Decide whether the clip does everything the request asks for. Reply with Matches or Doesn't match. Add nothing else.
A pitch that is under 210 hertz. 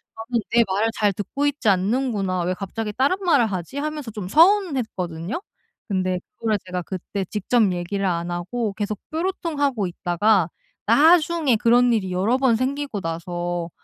Doesn't match